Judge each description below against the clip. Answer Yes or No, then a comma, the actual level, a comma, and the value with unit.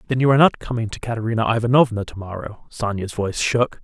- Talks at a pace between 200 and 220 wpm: Yes, fast, 205 wpm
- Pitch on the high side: No, low, 115 Hz